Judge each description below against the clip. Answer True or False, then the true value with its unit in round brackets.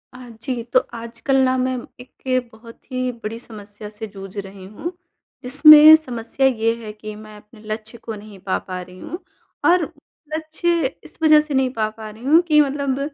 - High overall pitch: True (235 Hz)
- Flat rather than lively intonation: False (4.1 semitones)